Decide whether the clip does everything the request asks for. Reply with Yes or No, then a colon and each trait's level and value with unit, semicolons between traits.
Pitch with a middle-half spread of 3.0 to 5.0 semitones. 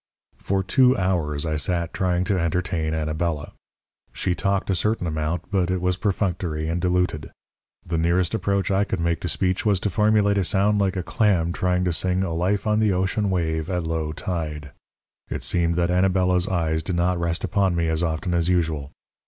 No: narrow, 2.6 semitones